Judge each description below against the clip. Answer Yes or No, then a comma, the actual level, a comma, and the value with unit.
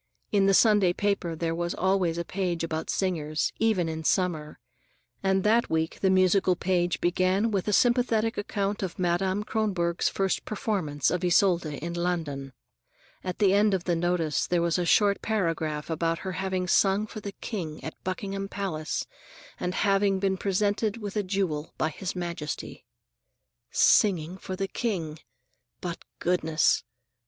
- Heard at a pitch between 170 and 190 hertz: Yes, medium, 185 Hz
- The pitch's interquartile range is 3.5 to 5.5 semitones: No, average, 2.9 semitones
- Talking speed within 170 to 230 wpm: No, average, 155 wpm